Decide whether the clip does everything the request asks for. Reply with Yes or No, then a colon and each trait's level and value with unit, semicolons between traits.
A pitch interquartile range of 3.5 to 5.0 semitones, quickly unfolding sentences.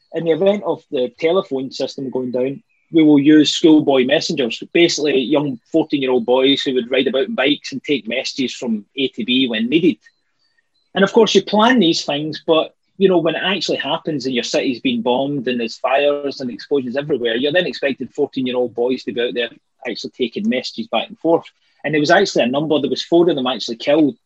Yes: average, 4.5 semitones; fast, 225 wpm